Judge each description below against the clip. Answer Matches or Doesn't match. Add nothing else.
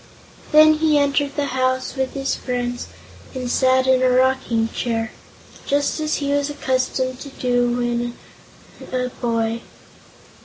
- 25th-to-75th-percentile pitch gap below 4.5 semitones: Matches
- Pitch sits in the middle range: Doesn't match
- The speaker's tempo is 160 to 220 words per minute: Doesn't match